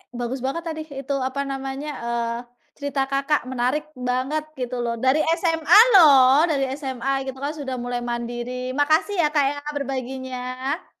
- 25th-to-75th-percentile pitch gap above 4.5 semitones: No, narrow, 2.5 semitones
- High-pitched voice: Yes, very high, 270 Hz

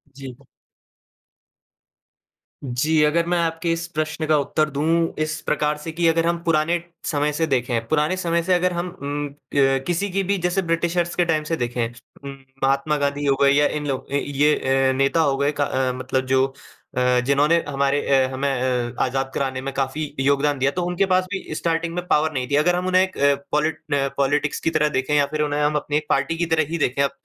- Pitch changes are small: No, average, 3.3 semitones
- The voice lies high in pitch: No, medium, 150 Hz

